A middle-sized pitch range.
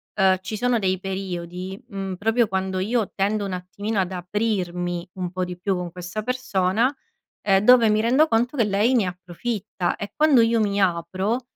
Yes: average, 3.6 semitones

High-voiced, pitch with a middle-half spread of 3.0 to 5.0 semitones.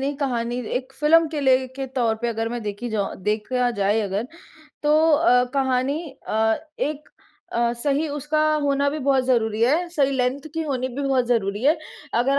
Yes: very high, 260 Hz; average, 3.4 semitones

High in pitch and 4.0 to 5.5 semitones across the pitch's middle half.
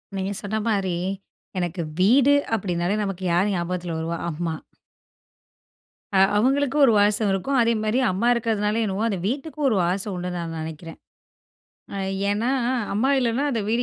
Yes: high, 205 Hz; average, 4.6 semitones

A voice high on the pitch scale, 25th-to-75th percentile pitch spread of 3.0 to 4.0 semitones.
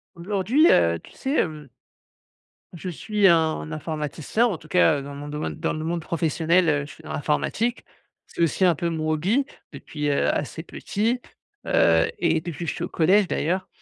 No: medium, 165 Hz; average, 3.6 semitones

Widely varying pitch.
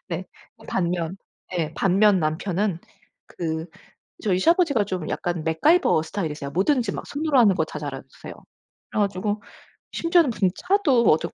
Yes: wide, 6.6 semitones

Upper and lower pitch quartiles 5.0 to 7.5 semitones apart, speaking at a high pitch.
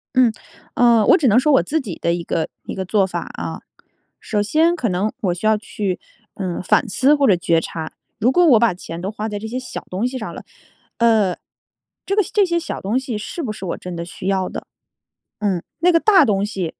Yes: wide, 5.6 semitones; high, 215 Hz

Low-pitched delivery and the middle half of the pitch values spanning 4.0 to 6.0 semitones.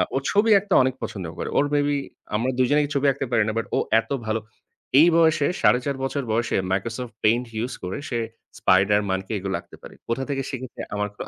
Yes: low, 125 Hz; average, 4.8 semitones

